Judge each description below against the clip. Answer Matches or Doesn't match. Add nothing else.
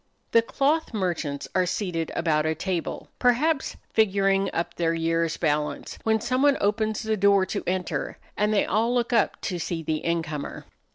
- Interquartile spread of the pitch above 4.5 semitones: Matches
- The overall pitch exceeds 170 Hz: Matches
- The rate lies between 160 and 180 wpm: Matches